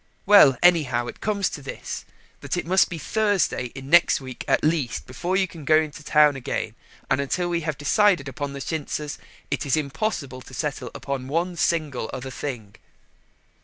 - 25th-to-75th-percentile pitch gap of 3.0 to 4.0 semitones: No, average, 4.4 semitones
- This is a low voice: No, medium, 150 Hz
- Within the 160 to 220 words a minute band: Yes, average, 180 wpm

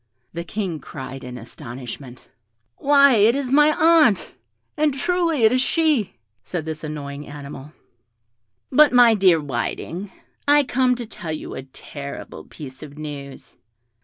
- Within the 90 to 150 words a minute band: Yes, average, 140 wpm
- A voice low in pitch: No, medium, 175 Hz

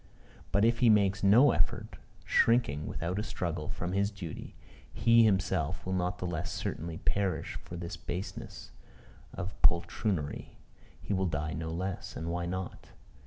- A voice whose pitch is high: No, very low, 90 Hz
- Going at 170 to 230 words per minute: No, average, 155 wpm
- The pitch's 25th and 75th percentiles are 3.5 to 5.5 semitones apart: No, average, 3.1 semitones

